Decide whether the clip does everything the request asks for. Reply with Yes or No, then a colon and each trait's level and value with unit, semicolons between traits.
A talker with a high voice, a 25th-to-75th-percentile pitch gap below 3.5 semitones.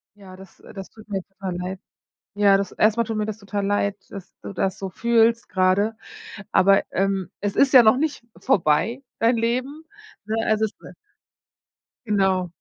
Yes: high, 205 Hz; average, 2.8 semitones